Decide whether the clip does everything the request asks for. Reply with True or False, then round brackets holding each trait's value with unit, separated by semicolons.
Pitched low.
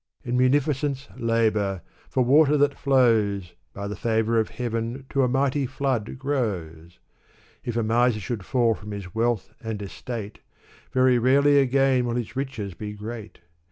True (120 Hz)